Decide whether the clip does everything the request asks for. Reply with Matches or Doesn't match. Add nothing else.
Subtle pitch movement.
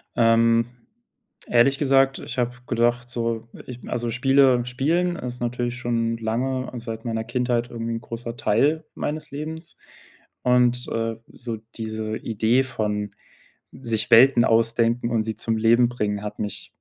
Matches